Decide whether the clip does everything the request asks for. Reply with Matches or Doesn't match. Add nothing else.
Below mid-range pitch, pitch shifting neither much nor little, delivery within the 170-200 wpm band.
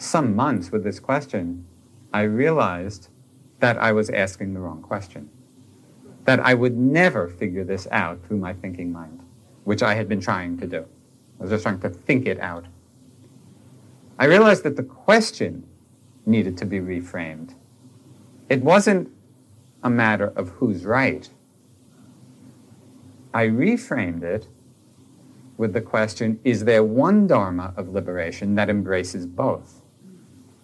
Doesn't match